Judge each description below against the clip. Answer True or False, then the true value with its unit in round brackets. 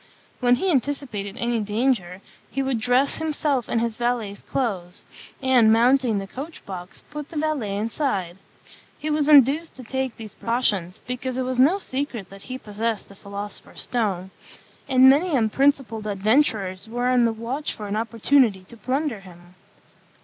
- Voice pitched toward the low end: False (240 Hz)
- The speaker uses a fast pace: False (160 wpm)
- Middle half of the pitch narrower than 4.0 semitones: False (4.6 semitones)